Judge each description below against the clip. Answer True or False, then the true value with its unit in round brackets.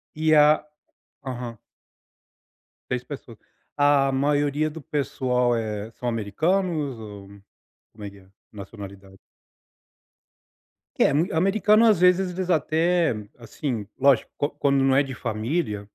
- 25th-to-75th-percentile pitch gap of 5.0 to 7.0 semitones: True (5.6 semitones)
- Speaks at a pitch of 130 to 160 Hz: True (135 Hz)